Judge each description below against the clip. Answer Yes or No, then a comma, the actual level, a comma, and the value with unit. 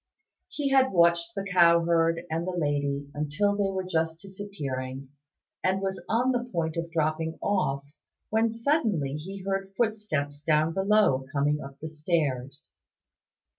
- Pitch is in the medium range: Yes, medium, 170 Hz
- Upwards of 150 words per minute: No, average, 145 wpm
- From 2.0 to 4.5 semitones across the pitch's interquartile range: No, average, 4.9 semitones